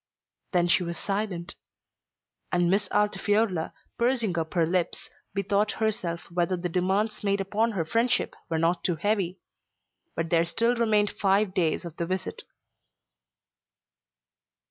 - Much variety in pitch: No, average, 3.4 semitones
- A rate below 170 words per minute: Yes, slow, 135 wpm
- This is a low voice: No, medium, 185 Hz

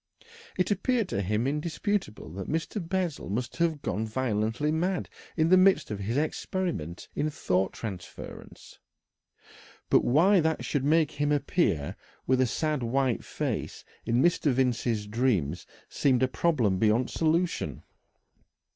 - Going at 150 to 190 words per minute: No, average, 140 wpm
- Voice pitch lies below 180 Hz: Yes, low, 135 Hz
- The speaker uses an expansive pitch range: Yes, wide, 6.8 semitones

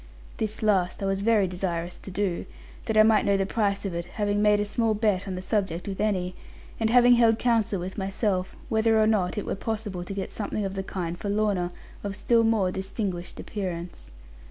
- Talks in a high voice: Yes, high, 200 Hz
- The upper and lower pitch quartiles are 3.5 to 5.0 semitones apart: No, average, 2.7 semitones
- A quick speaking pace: Yes, fast, 210 wpm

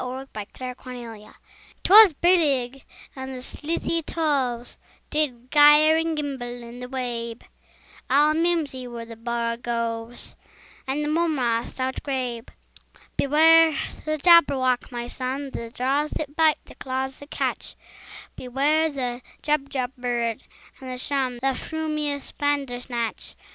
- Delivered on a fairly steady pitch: No, average, 3.6 semitones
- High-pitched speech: Yes, very high, 265 Hz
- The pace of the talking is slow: Yes, slow, 120 wpm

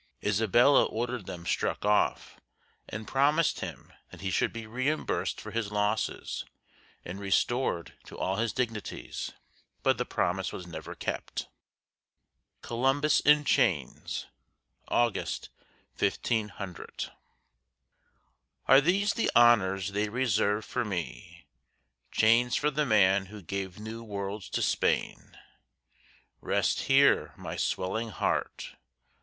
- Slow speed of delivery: Yes, slow, 115 wpm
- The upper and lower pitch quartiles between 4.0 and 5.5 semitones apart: Yes, average, 4.3 semitones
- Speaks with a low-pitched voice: Yes, low, 110 Hz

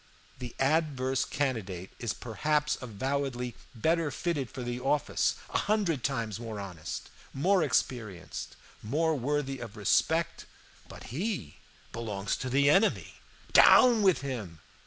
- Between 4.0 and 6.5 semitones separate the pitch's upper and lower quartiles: Yes, average, 4.9 semitones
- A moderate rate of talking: No, slow, 125 wpm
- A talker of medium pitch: No, low, 130 Hz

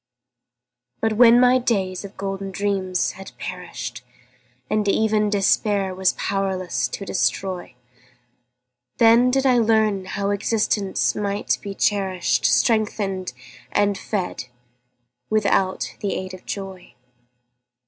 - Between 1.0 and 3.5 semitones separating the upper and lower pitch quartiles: Yes, narrow, 2.4 semitones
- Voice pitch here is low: No, high, 195 Hz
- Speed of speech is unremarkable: No, slow, 110 wpm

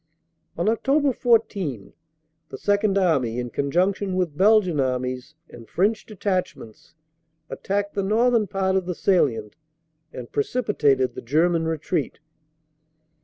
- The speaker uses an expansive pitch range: Yes, wide, 6.5 semitones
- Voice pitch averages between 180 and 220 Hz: Yes, medium, 185 Hz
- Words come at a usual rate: No, slow, 120 wpm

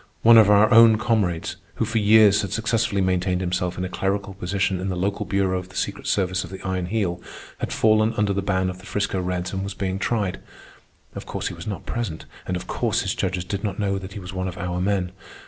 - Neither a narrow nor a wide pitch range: No, narrow, 2.1 semitones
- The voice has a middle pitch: No, very low, 95 Hz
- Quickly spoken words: Yes, fast, 240 wpm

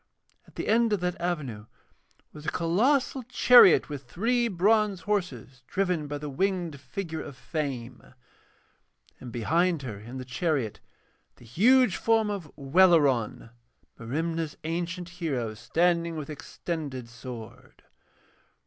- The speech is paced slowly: Yes, slow, 125 wpm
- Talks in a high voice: No, medium, 165 Hz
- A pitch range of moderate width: No, wide, 6.0 semitones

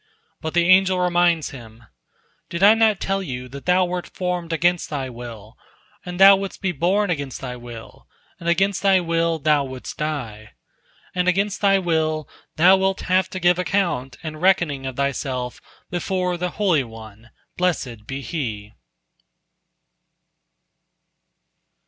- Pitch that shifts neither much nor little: No, wide, 5.7 semitones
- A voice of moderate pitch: Yes, medium, 170 Hz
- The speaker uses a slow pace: No, average, 145 wpm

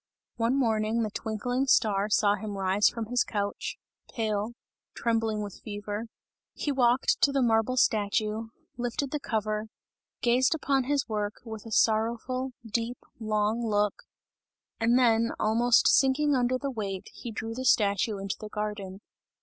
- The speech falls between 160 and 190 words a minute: No, average, 150 wpm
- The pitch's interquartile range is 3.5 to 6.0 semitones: No, average, 2.7 semitones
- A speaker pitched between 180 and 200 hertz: No, high, 225 Hz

